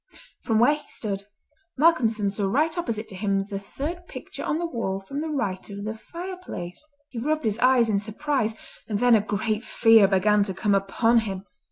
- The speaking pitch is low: No, high, 220 Hz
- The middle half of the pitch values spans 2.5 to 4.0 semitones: No, wide, 5.6 semitones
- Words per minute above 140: Yes, average, 195 wpm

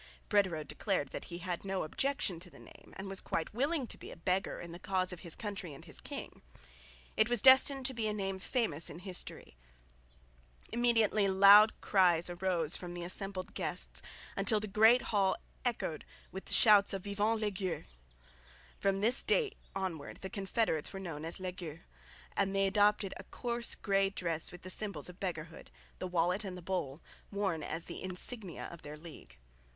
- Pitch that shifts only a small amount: No, average, 3.2 semitones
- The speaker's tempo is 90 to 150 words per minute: No, average, 185 wpm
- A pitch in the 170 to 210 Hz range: Yes, high, 190 Hz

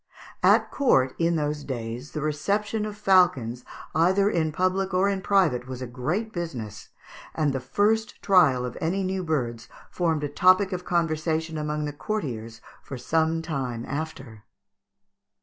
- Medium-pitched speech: Yes, medium, 160 Hz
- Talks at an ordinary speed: Yes, average, 150 wpm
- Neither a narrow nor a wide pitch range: No, wide, 6.0 semitones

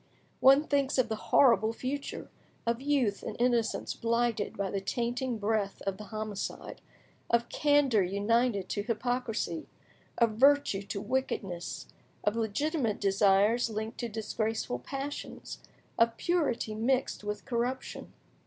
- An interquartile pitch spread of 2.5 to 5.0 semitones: Yes, average, 3.6 semitones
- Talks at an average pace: No, slow, 125 wpm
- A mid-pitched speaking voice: No, high, 230 Hz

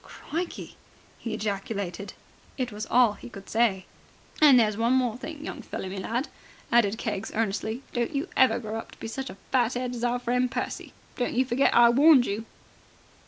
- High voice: Yes, high, 235 Hz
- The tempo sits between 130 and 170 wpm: No, average, 185 wpm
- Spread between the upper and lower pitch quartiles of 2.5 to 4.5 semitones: Yes, average, 2.9 semitones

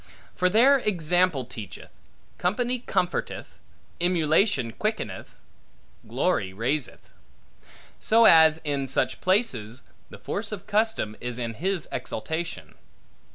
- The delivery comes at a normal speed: No, slow, 105 wpm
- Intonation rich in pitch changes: Yes, wide, 8.5 semitones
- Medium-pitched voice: Yes, medium, 170 Hz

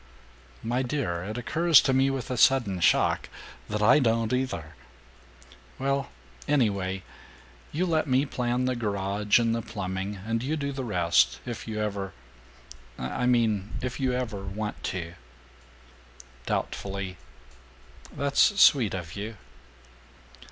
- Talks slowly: Yes, slow, 130 wpm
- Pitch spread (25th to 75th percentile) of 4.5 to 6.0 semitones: Yes, average, 5.0 semitones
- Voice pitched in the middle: No, low, 115 Hz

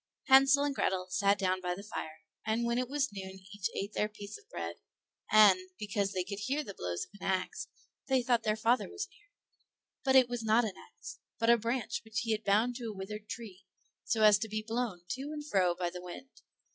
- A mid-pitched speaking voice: No, high, 215 Hz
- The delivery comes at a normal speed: No, fast, 225 wpm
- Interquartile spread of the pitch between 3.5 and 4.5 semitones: Yes, average, 4.0 semitones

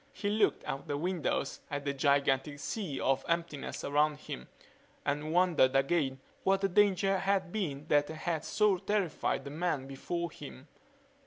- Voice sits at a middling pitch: Yes, medium, 155 Hz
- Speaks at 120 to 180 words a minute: Yes, average, 155 wpm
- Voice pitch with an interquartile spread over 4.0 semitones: Yes, average, 4.9 semitones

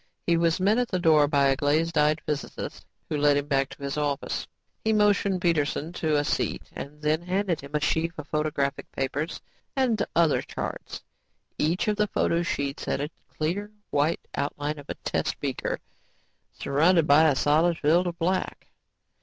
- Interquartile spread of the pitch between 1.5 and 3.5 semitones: Yes, average, 3.1 semitones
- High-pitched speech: No, medium, 155 Hz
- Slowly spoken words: No, average, 180 wpm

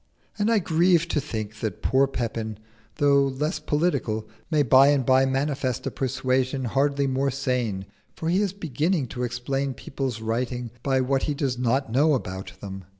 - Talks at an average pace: Yes, average, 170 wpm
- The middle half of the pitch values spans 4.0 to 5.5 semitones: No, average, 2.9 semitones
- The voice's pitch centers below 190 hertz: Yes, low, 135 Hz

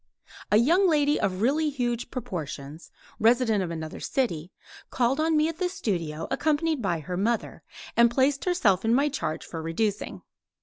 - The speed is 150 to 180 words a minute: Yes, average, 165 wpm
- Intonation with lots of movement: Yes, wide, 8.4 semitones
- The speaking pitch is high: Yes, high, 235 Hz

